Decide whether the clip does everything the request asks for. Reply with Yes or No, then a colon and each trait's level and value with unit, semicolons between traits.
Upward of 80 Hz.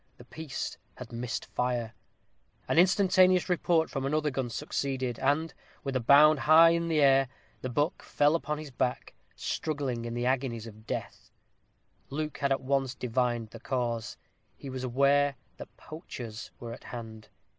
Yes: low, 135 Hz